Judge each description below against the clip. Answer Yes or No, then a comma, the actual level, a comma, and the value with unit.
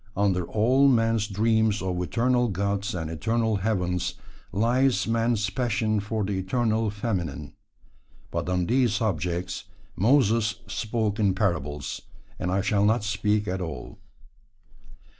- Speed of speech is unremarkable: No, slow, 125 wpm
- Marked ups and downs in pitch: No, average, 3.4 semitones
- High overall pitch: No, low, 105 Hz